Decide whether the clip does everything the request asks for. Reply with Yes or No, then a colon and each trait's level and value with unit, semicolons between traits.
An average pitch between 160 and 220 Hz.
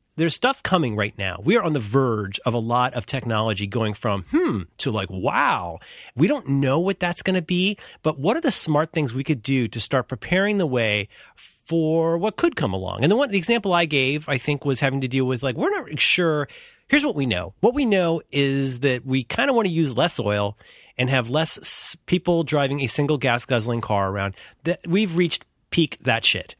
No: medium, 140 Hz